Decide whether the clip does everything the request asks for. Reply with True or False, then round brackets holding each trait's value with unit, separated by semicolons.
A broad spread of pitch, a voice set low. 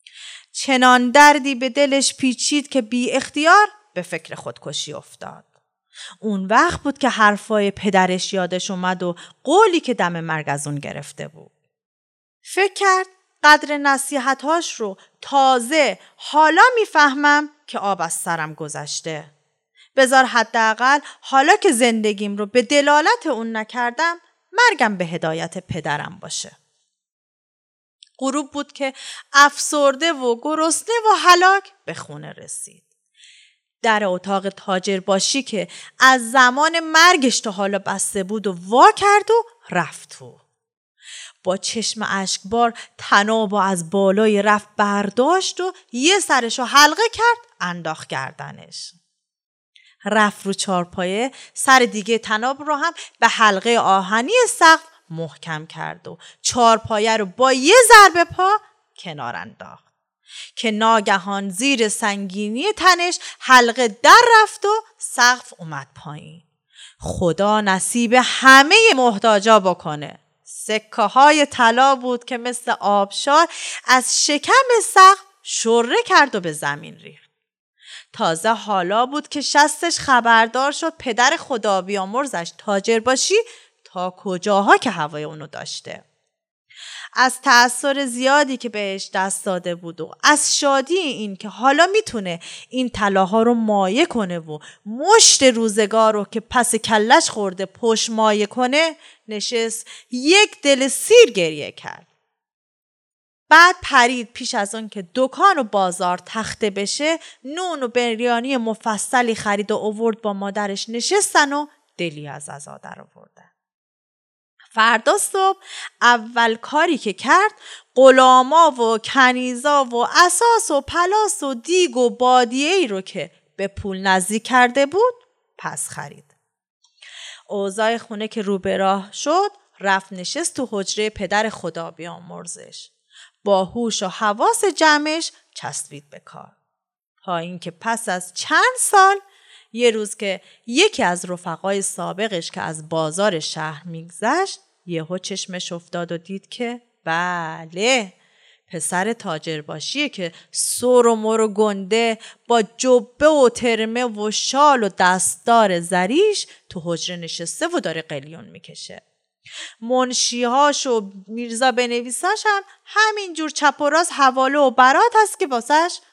False (7.1 semitones; 235 Hz)